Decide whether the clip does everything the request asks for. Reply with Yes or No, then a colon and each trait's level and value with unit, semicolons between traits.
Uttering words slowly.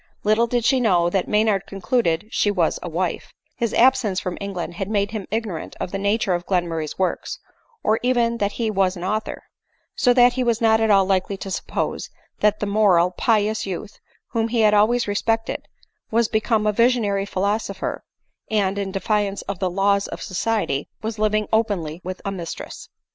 No: average, 185 wpm